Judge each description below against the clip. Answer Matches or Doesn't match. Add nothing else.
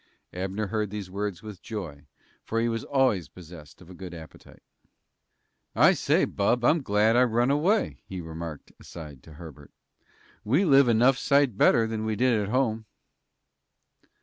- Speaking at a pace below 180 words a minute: Matches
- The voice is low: Matches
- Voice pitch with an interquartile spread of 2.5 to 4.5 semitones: Doesn't match